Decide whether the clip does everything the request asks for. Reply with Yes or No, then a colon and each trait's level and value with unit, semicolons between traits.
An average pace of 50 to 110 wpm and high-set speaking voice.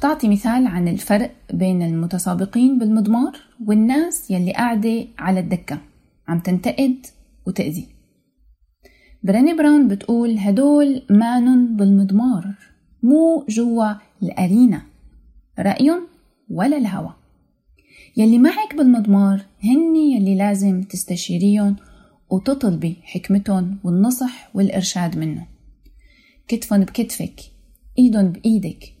Yes: average, 90 wpm; high, 205 Hz